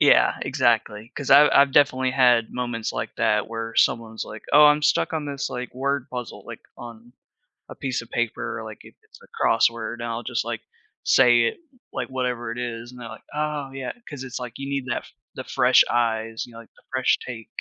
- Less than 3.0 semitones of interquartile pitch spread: Yes, narrow, 2.5 semitones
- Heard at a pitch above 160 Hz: No, low, 120 Hz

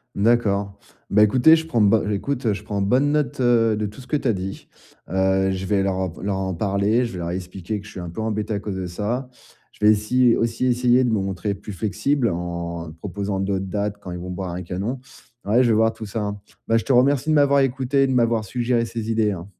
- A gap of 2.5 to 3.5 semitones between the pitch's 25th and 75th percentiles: No, average, 3.9 semitones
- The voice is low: Yes, low, 105 Hz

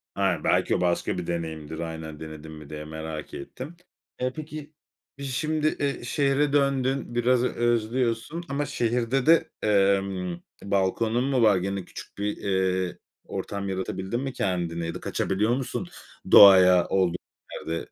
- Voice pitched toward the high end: No, low, 100 Hz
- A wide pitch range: Yes, wide, 6.5 semitones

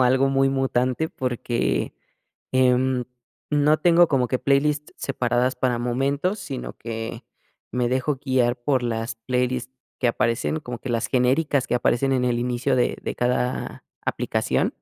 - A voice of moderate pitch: No, low, 130 Hz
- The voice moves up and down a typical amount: No, narrow, 1.9 semitones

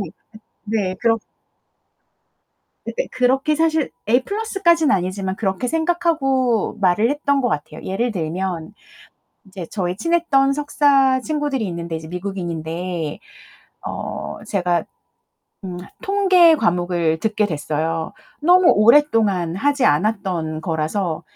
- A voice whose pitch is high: Yes, high, 210 Hz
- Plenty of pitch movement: Yes, wide, 8.4 semitones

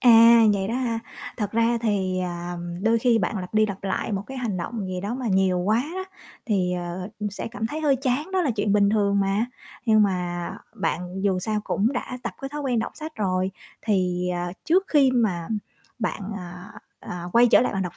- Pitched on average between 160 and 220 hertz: Yes, high, 210 Hz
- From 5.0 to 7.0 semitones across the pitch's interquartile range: No, average, 4.2 semitones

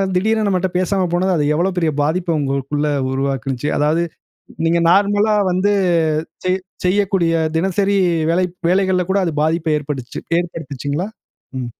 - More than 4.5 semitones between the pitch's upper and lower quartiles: No, average, 4.2 semitones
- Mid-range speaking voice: Yes, medium, 170 Hz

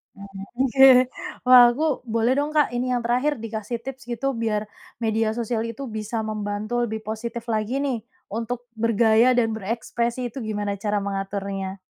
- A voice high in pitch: Yes, high, 230 Hz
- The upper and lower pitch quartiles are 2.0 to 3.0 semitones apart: Yes, narrow, 2.4 semitones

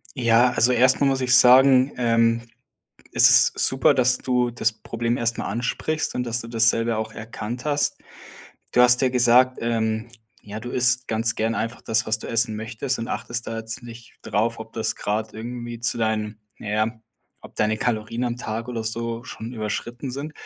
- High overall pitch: No, low, 115 Hz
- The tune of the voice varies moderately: No, narrow, 1.9 semitones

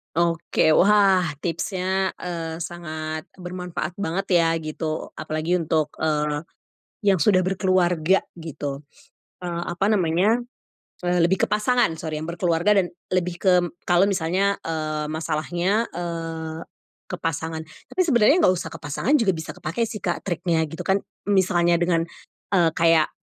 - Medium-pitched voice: Yes, medium, 175 Hz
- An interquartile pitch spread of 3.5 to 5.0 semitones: No, average, 2.7 semitones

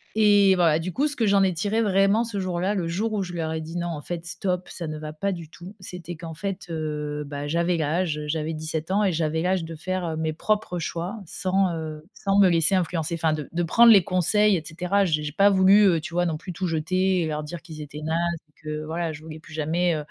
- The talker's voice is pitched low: No, medium, 170 Hz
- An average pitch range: Yes, average, 3.2 semitones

